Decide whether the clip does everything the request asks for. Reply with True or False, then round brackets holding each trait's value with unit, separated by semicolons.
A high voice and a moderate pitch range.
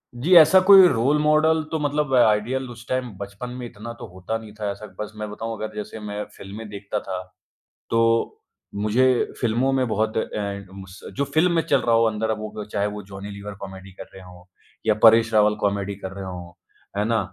False (110 Hz; 3.3 semitones)